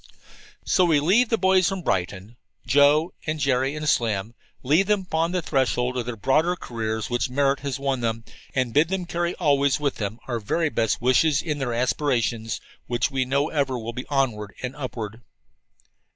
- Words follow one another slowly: No, average, 180 wpm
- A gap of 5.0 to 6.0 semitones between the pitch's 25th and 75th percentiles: No, average, 4.6 semitones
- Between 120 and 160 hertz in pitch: Yes, low, 135 Hz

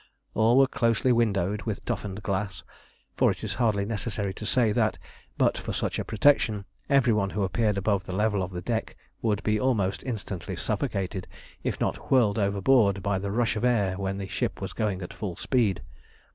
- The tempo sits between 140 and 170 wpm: No, average, 190 wpm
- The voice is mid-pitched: No, low, 105 Hz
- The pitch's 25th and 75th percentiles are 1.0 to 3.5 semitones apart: Yes, average, 2.9 semitones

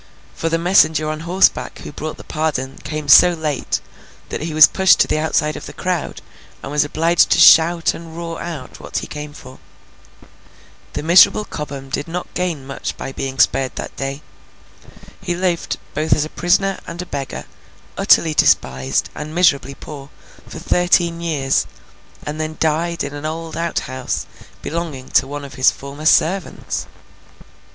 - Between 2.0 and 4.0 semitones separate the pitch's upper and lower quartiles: Yes, average, 3.1 semitones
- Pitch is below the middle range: No, medium, 155 Hz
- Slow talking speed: No, average, 165 wpm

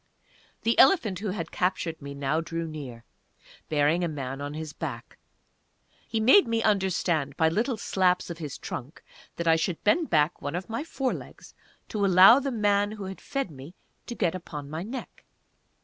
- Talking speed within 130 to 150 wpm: No, average, 180 wpm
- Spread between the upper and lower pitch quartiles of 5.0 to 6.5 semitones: Yes, wide, 5.5 semitones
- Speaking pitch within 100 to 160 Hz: No, medium, 175 Hz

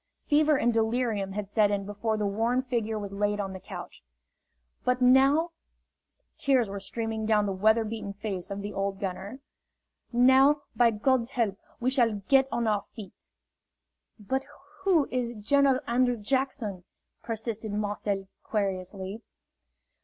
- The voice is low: No, high, 220 Hz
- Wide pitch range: No, average, 3.7 semitones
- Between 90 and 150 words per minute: Yes, average, 145 wpm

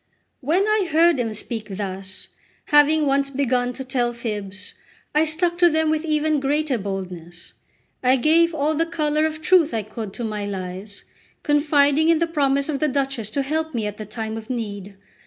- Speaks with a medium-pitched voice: No, very high, 275 Hz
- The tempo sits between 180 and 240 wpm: Yes, average, 185 wpm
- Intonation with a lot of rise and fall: Yes, wide, 6.3 semitones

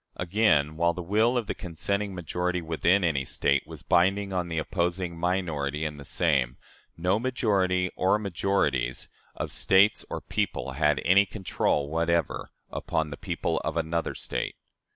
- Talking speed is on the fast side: No, average, 150 wpm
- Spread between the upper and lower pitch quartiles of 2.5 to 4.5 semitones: Yes, average, 3.7 semitones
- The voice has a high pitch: No, very low, 90 Hz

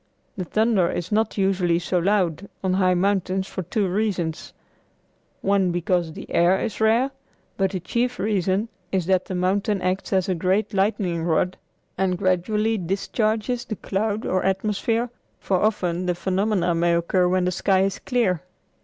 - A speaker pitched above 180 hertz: Yes, high, 190 Hz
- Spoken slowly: No, average, 165 wpm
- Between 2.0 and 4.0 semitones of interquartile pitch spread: Yes, average, 2.7 semitones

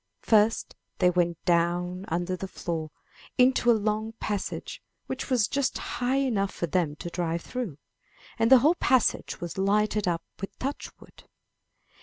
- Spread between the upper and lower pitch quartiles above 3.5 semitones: Yes, average, 5.2 semitones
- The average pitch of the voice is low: No, high, 195 Hz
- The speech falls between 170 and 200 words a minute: No, average, 155 wpm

